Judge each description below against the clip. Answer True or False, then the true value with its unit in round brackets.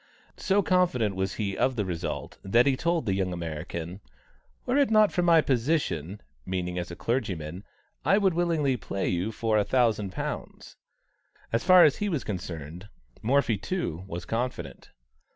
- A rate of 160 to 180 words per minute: True (165 wpm)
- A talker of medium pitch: False (110 Hz)